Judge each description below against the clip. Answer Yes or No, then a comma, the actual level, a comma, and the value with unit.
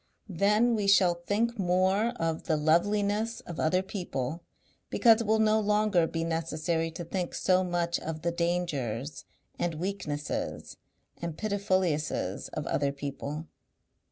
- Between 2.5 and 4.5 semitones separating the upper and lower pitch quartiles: Yes, average, 4.2 semitones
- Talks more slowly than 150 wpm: Yes, slow, 135 wpm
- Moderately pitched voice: Yes, medium, 175 Hz